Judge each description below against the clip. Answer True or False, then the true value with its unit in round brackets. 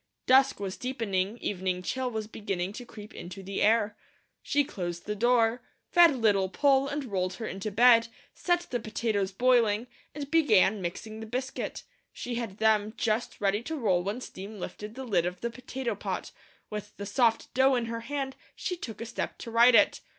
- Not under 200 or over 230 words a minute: False (185 wpm)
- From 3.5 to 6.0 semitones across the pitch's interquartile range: True (3.8 semitones)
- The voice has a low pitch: False (225 Hz)